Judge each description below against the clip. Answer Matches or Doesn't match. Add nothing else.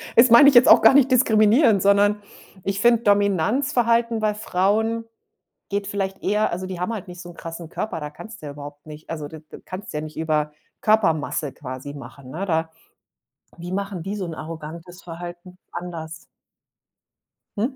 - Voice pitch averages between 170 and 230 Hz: Matches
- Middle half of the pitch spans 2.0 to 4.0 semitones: Doesn't match